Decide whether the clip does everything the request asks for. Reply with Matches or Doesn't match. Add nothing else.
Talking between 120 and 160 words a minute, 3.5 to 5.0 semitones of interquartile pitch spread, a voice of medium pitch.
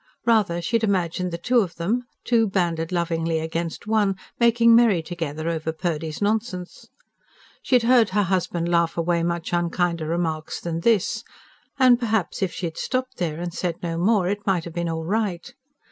Doesn't match